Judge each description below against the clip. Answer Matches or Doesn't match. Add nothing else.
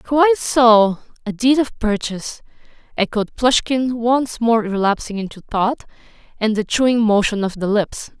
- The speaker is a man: Doesn't match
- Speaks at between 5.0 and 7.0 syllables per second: Doesn't match